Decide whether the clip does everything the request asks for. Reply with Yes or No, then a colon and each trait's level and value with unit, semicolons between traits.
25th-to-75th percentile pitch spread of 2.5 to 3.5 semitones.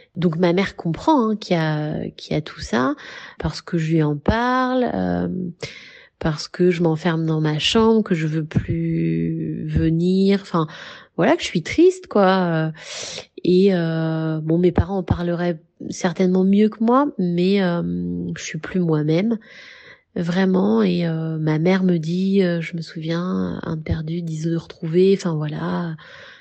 Yes: average, 3.1 semitones